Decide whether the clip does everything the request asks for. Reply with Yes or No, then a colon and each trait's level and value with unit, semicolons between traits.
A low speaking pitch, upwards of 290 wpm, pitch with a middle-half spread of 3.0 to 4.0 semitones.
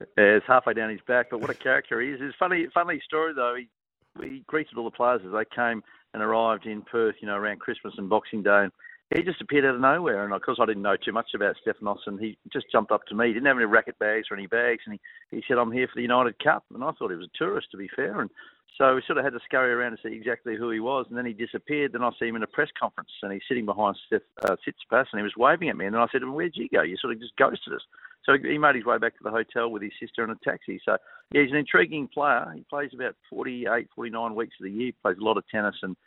Yes: low, 120 Hz; fast, 300 wpm; average, 3.5 semitones